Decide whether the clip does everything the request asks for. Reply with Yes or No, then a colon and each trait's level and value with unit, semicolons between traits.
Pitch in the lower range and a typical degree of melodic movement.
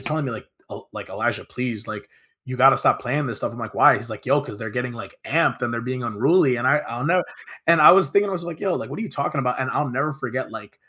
Yes: low, 130 Hz; average, 4.3 semitones